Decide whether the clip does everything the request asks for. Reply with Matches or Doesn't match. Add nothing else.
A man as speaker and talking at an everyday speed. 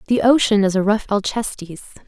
Doesn't match